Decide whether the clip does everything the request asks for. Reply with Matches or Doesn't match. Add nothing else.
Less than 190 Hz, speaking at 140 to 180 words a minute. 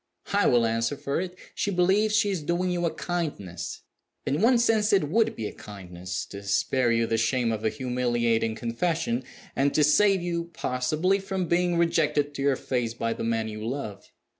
Doesn't match